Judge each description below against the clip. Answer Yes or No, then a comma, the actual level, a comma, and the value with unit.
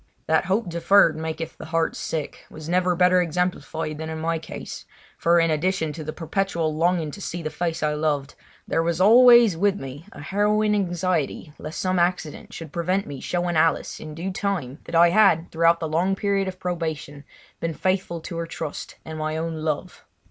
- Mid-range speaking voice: Yes, medium, 165 Hz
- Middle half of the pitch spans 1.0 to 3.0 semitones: Yes, average, 2.7 semitones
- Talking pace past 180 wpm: Yes, average, 190 wpm